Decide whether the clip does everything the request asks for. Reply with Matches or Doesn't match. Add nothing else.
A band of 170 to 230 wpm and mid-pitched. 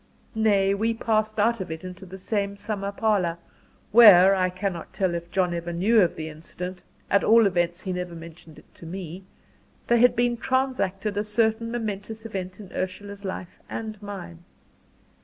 Doesn't match